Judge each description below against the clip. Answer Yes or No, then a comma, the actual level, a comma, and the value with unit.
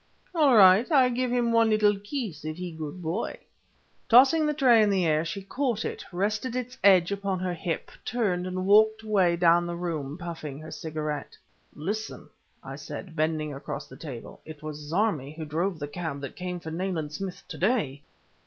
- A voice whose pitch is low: No, medium, 180 Hz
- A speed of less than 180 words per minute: No, average, 190 wpm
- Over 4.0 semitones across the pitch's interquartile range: Yes, wide, 5.6 semitones